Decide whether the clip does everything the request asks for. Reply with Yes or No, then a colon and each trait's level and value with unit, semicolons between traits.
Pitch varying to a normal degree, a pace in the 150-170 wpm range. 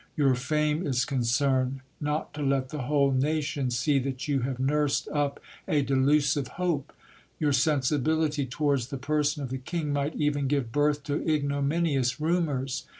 No: narrow, 2.2 semitones; average, 155 wpm